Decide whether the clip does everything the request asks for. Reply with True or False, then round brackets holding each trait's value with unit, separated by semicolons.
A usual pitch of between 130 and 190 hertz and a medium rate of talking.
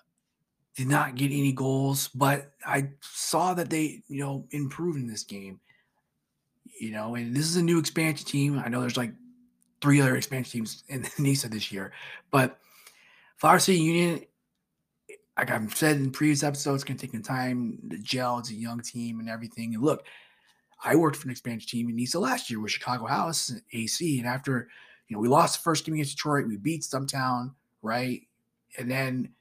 True (135 Hz; 190 wpm)